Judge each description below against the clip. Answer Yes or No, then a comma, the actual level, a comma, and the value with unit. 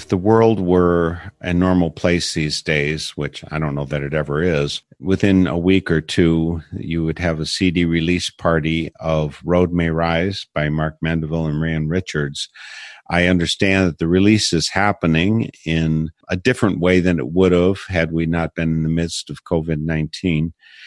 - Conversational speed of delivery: Yes, average, 180 wpm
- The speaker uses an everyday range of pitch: No, narrow, 2.3 semitones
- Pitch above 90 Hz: No, very low, 85 Hz